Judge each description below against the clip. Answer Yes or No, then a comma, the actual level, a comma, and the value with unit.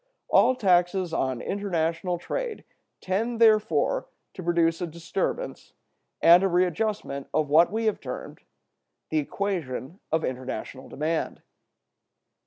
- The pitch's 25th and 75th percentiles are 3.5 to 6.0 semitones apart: Yes, average, 4.1 semitones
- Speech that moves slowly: Yes, slow, 115 wpm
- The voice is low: No, medium, 175 Hz